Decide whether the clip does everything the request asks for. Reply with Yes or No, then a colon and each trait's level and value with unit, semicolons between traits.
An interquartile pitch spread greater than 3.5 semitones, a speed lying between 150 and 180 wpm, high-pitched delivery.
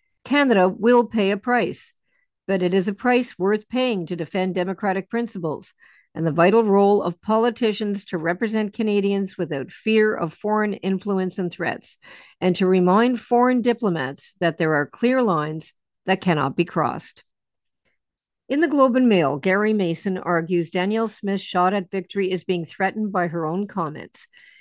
Yes: average, 3.9 semitones; average, 160 wpm; high, 195 Hz